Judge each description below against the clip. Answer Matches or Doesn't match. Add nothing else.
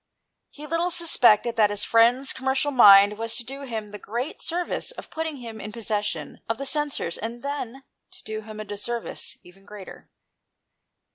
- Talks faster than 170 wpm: Matches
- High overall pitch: Matches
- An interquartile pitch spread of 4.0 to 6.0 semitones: Matches